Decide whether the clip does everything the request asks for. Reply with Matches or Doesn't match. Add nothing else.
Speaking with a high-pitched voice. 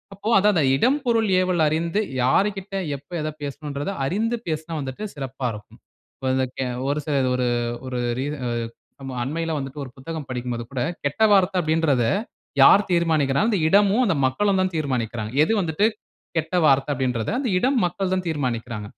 Doesn't match